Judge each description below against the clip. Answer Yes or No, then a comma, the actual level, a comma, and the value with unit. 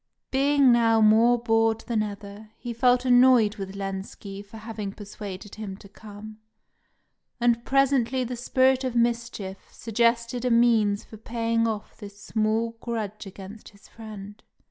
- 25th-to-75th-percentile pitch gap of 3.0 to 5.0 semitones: No, narrow, 2.6 semitones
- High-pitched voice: Yes, high, 225 Hz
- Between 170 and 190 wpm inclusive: No, average, 145 wpm